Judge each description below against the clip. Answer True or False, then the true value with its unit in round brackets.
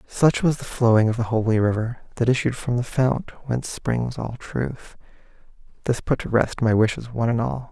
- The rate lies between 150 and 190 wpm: False (200 wpm)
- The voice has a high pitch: False (120 Hz)